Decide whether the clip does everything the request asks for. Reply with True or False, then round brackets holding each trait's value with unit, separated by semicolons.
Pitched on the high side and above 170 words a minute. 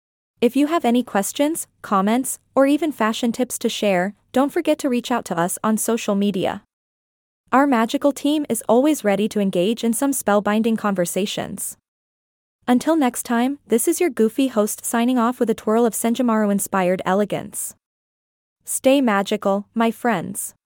False (230 Hz; 155 wpm)